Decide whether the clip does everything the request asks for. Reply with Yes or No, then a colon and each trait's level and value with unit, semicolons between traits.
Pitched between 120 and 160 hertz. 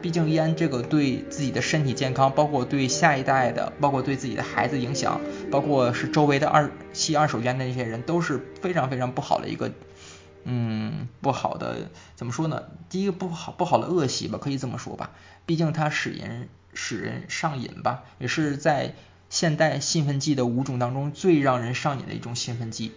Yes: medium, 140 Hz